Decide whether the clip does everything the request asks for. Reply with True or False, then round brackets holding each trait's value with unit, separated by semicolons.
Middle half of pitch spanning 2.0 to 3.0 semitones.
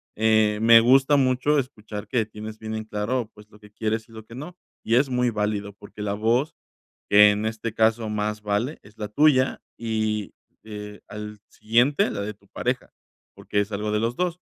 True (2.5 semitones)